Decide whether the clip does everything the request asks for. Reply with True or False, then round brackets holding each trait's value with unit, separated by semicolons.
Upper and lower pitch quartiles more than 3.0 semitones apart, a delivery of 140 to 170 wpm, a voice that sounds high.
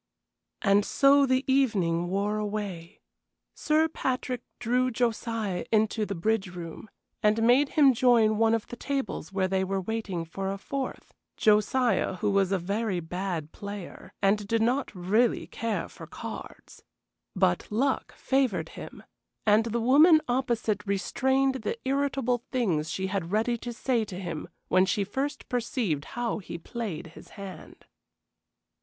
True (4.5 semitones; 150 wpm; 215 Hz)